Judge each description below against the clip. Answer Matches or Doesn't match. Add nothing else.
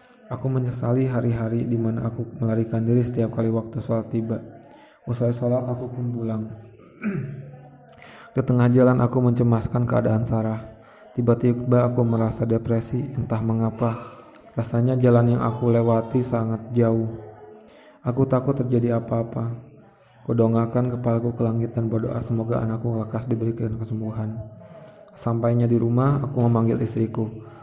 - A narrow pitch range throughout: Matches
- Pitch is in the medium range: Doesn't match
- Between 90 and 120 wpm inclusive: Doesn't match